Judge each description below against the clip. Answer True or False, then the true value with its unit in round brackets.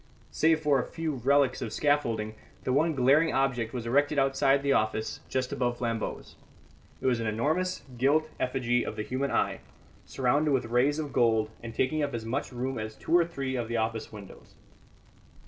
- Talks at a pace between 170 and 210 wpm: True (185 wpm)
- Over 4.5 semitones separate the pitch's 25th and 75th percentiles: False (3.6 semitones)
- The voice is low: True (130 Hz)